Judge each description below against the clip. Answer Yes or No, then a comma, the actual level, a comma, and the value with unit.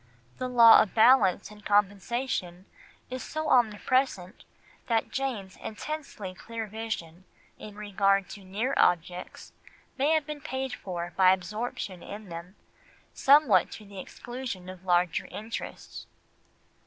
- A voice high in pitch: Yes, high, 210 Hz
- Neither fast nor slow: No, slow, 125 wpm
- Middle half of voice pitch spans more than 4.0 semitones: Yes, average, 5.0 semitones